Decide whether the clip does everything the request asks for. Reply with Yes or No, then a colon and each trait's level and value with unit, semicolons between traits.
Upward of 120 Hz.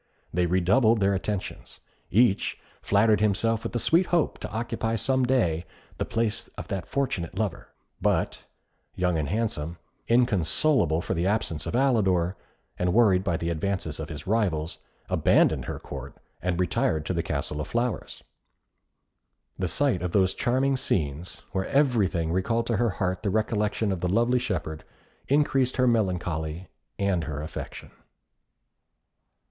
No: low, 100 Hz